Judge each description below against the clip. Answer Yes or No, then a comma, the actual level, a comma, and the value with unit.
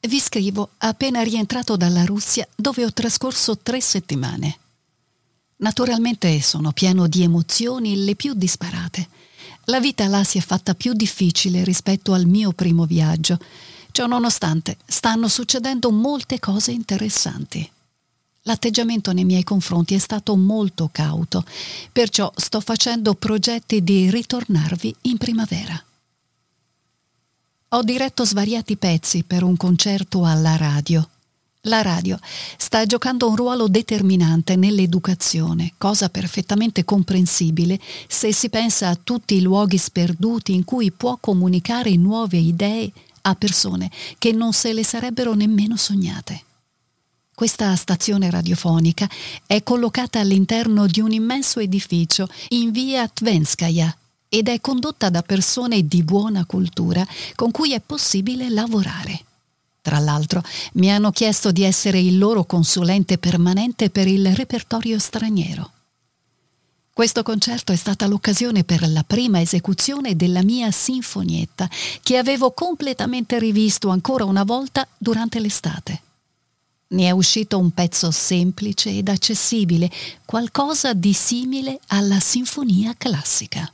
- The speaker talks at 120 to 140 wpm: Yes, average, 125 wpm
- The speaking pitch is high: Yes, high, 200 Hz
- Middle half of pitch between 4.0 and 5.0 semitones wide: Yes, average, 4.5 semitones